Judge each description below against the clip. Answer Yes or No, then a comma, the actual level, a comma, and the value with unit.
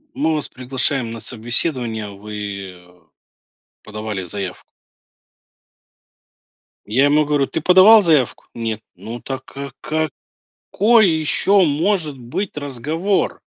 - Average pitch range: No, wide, 6.6 semitones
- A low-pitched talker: Yes, low, 130 Hz